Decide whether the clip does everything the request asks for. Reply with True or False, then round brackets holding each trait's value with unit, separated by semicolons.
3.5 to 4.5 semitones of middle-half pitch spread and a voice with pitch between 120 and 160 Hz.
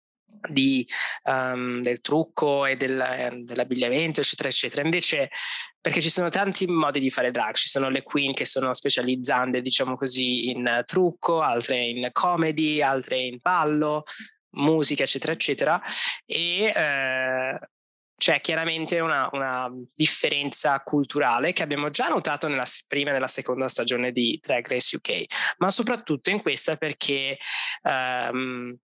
True (3.9 semitones; 140 Hz)